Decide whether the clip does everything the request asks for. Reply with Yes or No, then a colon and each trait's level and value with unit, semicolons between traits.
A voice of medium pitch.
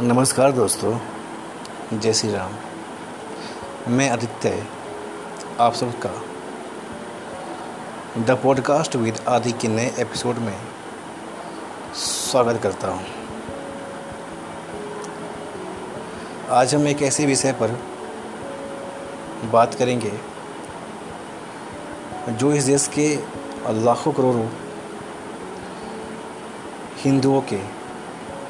No: low, 120 Hz